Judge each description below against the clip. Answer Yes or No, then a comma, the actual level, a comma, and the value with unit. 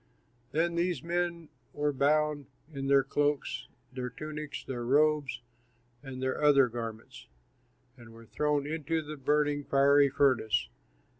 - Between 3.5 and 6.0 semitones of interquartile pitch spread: No, average, 2.7 semitones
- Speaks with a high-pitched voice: No, medium, 145 Hz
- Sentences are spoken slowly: Yes, slow, 130 wpm